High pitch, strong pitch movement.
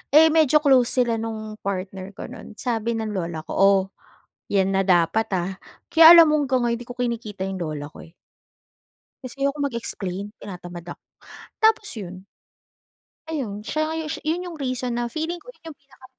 Yes: high, 230 Hz; wide, 6.8 semitones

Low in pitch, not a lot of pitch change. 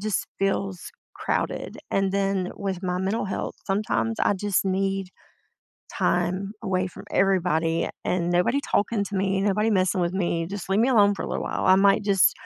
No: high, 195 Hz; narrow, 1.6 semitones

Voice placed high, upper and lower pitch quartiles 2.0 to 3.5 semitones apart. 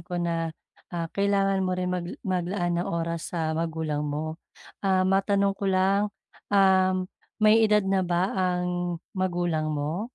No: medium, 180 Hz; narrow, 2.5 semitones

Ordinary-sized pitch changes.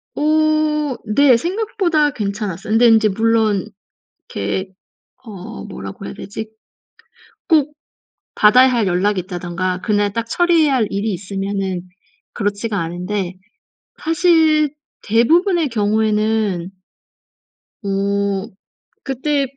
No: wide, 6.8 semitones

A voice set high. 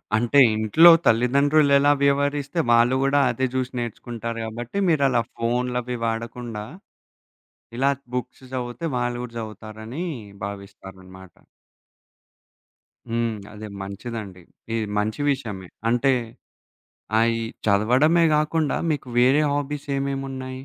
No: low, 120 Hz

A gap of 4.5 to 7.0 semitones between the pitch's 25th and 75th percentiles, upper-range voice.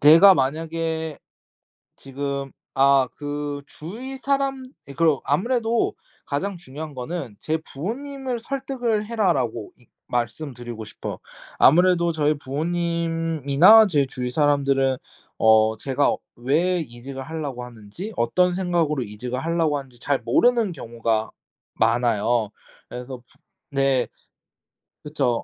No: wide, 5.6 semitones; medium, 145 Hz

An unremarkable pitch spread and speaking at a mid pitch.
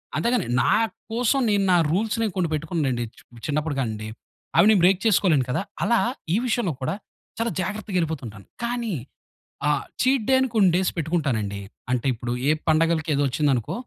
No: wide, 7.5 semitones; medium, 170 Hz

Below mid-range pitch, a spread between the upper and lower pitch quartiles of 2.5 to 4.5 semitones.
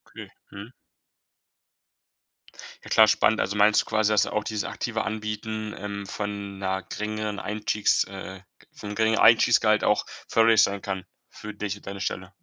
No: low, 105 Hz; narrow, 1.3 semitones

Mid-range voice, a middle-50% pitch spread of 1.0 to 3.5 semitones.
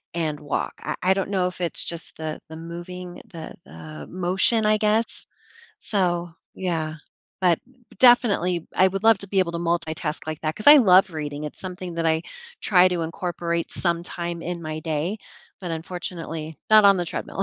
Yes: medium, 175 Hz; narrow, 2.6 semitones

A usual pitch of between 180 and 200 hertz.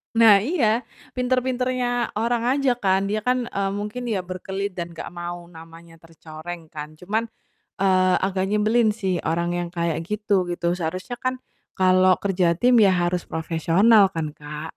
Yes: high, 190 Hz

